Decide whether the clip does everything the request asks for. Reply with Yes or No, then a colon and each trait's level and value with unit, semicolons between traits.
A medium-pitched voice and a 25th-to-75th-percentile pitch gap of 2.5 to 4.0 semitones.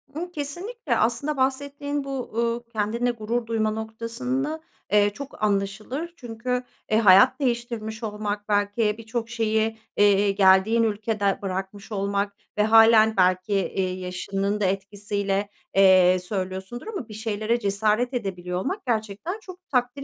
No: high, 220 Hz; average, 3.4 semitones